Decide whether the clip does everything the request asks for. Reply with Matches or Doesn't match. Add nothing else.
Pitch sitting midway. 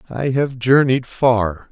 Doesn't match